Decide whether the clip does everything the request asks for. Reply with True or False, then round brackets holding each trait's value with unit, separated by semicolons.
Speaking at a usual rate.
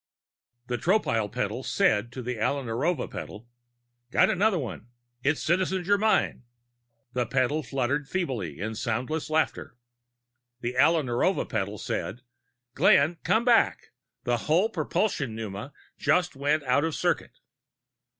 False (130 wpm)